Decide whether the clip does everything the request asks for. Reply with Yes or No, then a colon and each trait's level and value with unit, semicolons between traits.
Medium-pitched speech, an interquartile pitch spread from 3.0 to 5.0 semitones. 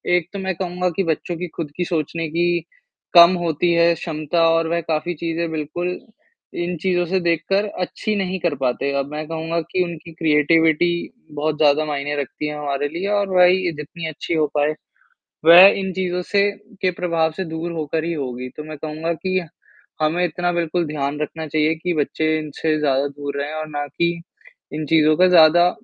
No: medium, 165 Hz; narrow, 2.4 semitones